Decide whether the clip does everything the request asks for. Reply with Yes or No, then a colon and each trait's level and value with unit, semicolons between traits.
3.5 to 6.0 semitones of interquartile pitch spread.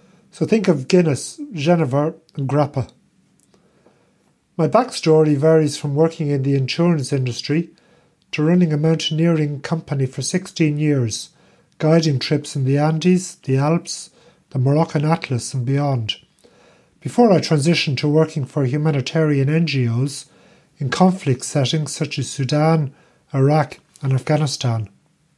No: average, 2.8 semitones